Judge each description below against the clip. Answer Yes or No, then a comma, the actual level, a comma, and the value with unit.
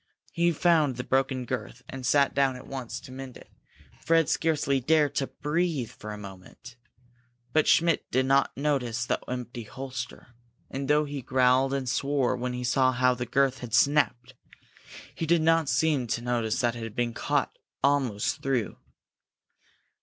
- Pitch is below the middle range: Yes, low, 130 Hz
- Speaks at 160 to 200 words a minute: Yes, average, 170 wpm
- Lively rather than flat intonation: No, average, 2.7 semitones